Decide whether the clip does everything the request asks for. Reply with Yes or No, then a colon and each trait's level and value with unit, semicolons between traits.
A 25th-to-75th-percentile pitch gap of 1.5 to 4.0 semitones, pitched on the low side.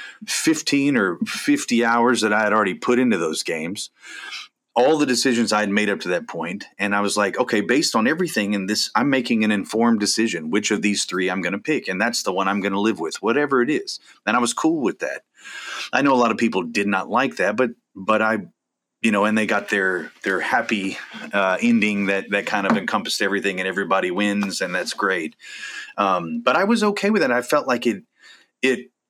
Yes: average, 3.7 semitones; low, 110 Hz